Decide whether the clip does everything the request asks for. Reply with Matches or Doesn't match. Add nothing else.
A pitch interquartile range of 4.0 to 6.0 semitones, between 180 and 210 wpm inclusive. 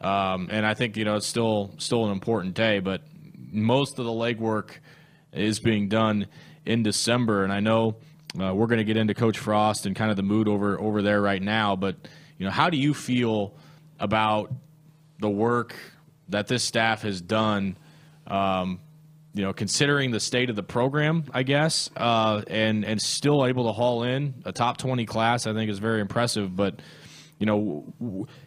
Matches